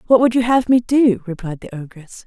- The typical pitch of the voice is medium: No, high, 215 Hz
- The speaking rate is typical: No, fast, 240 wpm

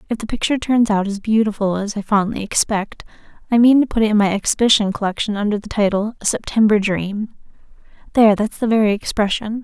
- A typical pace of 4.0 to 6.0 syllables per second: No, 6.2 syllables/s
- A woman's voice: Yes, female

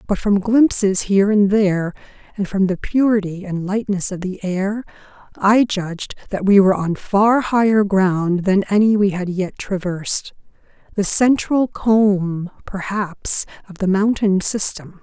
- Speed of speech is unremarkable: Yes, average, 150 wpm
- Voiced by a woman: Yes, female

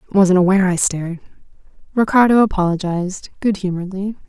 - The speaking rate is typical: No, slow, 110 wpm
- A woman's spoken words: Yes, female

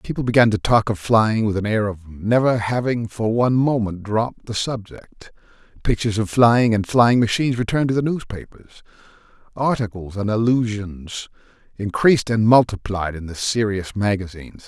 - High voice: No, low, 110 Hz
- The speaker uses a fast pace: No, average, 155 wpm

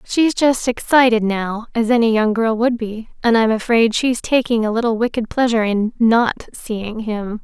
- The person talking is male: No, female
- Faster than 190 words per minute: No, average, 180 wpm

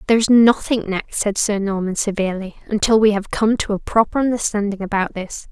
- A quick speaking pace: No, average, 195 wpm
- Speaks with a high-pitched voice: Yes, high, 210 Hz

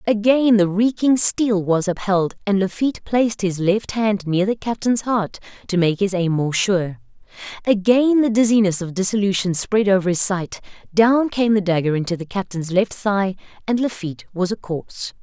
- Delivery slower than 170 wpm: No, average, 175 wpm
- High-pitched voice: Yes, high, 200 Hz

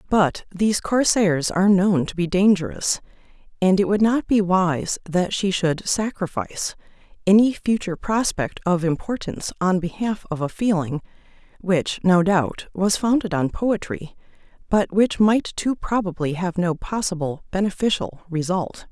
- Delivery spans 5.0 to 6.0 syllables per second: No, 4.5 syllables/s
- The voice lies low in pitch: No, medium, 185 Hz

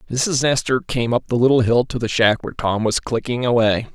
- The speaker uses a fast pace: Yes, fast, 230 wpm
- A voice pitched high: No, low, 120 Hz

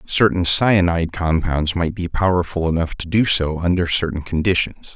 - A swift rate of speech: No, average, 155 wpm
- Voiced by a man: Yes, male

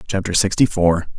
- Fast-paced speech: No, average, 150 wpm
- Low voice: Yes, very low, 95 Hz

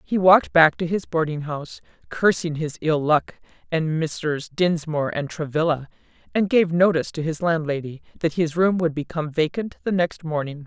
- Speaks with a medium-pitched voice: Yes, medium, 160 Hz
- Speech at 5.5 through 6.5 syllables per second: No, 5.1 syllables/s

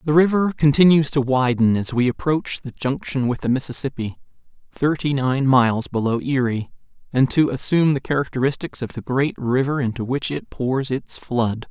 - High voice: No, low, 135 Hz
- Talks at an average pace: Yes, average, 160 wpm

